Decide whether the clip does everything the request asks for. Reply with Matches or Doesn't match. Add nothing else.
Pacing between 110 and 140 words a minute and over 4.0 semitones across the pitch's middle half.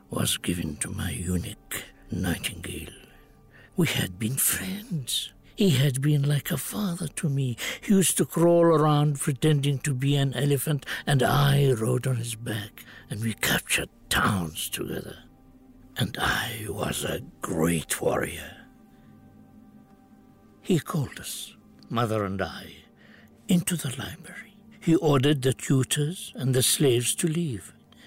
Matches